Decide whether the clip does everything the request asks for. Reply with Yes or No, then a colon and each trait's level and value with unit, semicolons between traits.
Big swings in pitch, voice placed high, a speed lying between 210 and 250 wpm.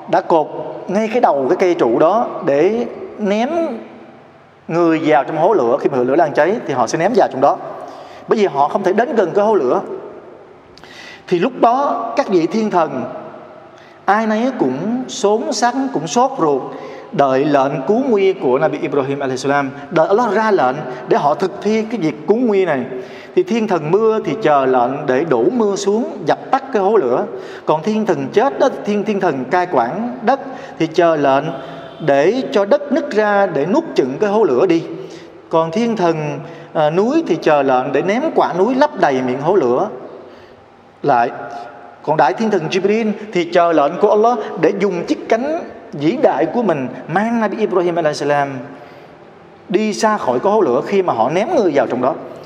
No: wide, 6.2 semitones; high, 195 Hz; average, 195 wpm